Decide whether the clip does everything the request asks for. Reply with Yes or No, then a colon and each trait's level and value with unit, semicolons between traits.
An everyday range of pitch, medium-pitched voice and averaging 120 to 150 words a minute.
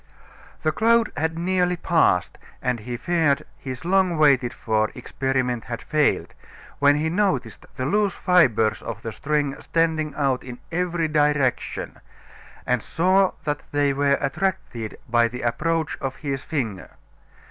Yes: average, 4.9 semitones; medium, 145 Hz; average, 140 wpm